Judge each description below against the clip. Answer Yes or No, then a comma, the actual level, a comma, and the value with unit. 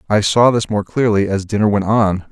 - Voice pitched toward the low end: Yes, low, 105 Hz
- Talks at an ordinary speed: No, fast, 235 wpm